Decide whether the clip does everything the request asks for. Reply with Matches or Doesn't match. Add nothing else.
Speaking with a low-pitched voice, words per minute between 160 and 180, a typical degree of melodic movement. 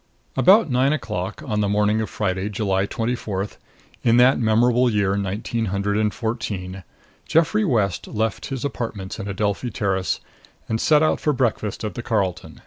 Matches